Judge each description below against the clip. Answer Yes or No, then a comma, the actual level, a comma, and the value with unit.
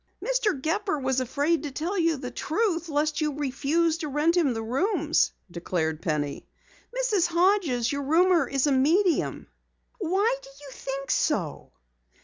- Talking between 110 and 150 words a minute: Yes, average, 145 wpm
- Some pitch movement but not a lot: Yes, average, 4.6 semitones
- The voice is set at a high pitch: Yes, very high, 305 Hz